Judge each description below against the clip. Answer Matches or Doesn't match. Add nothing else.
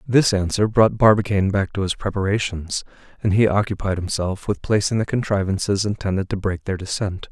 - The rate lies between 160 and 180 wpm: Matches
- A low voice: Matches